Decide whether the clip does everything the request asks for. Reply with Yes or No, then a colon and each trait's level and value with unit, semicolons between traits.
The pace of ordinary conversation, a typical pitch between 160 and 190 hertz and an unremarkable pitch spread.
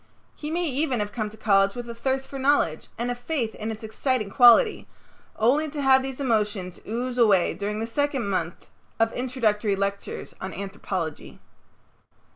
No: average, 170 wpm; high, 230 Hz; average, 4.3 semitones